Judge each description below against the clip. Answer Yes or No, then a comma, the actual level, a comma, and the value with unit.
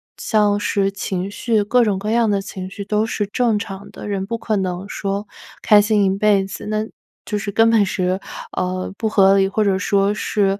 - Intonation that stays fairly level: Yes, narrow, 1.7 semitones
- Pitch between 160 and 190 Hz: No, high, 205 Hz